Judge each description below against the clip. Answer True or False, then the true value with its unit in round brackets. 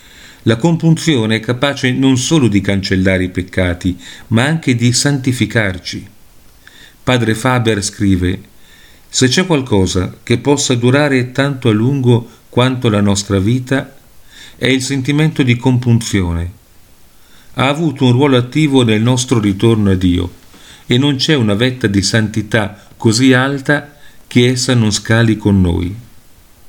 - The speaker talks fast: False (135 wpm)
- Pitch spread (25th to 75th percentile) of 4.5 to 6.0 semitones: True (4.8 semitones)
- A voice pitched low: True (120 Hz)